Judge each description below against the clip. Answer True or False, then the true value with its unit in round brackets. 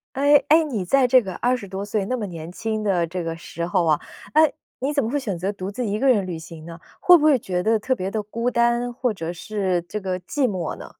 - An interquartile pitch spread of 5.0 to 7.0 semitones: True (5.5 semitones)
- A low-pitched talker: False (210 Hz)